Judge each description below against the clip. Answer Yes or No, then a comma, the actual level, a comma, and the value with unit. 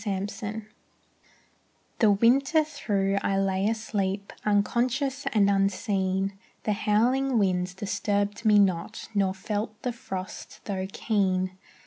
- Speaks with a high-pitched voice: Yes, high, 205 Hz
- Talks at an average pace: No, slow, 115 wpm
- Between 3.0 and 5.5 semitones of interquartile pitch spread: No, narrow, 2.6 semitones